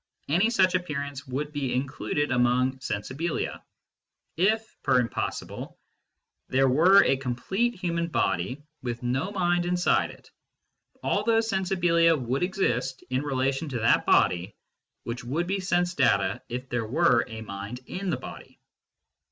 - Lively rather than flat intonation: Yes, wide, 6.1 semitones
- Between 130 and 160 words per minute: Yes, average, 145 wpm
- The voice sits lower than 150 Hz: Yes, medium, 140 Hz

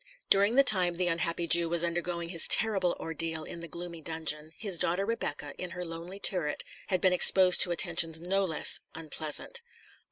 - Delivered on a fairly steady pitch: Yes, narrow, 2.1 semitones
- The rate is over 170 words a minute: Yes, average, 180 wpm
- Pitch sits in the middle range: Yes, medium, 170 Hz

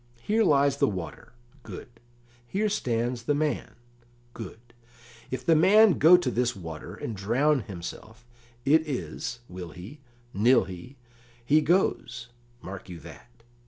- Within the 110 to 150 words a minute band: Yes, slow, 135 wpm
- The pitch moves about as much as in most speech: No, wide, 6.2 semitones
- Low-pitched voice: Yes, low, 125 Hz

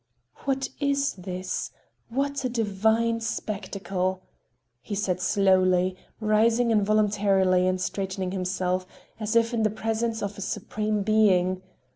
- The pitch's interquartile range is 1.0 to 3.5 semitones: Yes, average, 3.2 semitones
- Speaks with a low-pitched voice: No, high, 205 Hz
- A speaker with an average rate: No, slow, 120 wpm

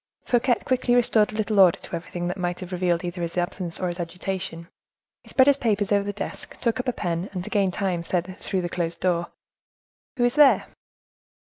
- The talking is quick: Yes, fast, 210 wpm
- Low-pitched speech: No, medium, 185 Hz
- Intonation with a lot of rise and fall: No, average, 3.7 semitones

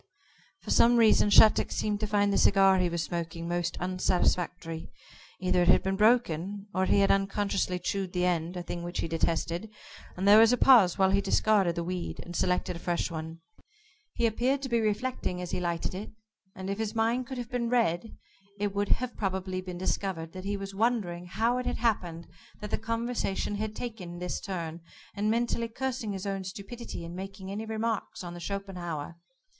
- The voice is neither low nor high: No, high, 195 Hz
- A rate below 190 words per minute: No, average, 195 wpm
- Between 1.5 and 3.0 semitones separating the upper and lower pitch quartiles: No, average, 3.8 semitones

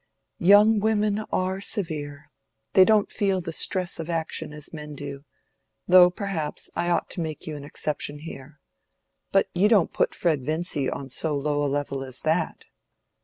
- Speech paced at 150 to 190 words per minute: Yes, average, 170 wpm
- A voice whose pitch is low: No, medium, 160 Hz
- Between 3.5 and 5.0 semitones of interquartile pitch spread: Yes, average, 4.4 semitones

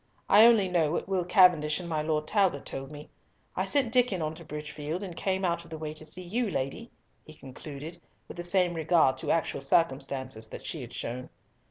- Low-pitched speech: No, medium, 165 Hz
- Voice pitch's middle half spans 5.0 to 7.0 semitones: No, average, 3.5 semitones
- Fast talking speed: Yes, fast, 210 wpm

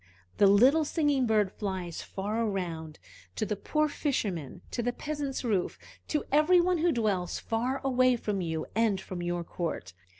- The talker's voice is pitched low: No, high, 220 Hz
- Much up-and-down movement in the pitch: Yes, wide, 6.6 semitones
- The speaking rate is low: No, average, 165 wpm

